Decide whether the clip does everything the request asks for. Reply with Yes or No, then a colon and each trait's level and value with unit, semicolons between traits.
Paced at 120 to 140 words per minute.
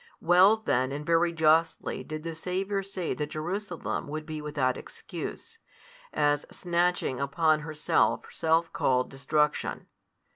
Yes: slow, 135 wpm